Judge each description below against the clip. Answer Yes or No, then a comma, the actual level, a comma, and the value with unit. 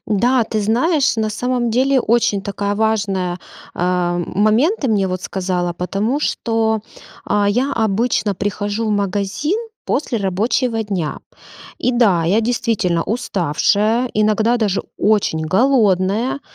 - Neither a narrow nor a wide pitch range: Yes, average, 3.6 semitones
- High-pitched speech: Yes, high, 215 Hz